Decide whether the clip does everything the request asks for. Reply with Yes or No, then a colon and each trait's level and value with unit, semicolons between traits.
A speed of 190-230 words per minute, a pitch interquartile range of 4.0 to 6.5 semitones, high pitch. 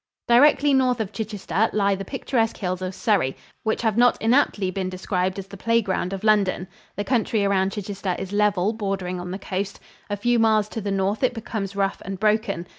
No: average, 200 wpm; average, 2.7 semitones; high, 205 Hz